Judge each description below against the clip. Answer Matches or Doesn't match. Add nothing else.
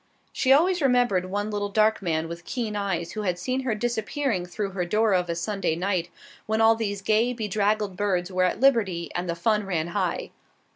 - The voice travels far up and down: Doesn't match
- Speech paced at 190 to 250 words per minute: Matches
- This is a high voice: Matches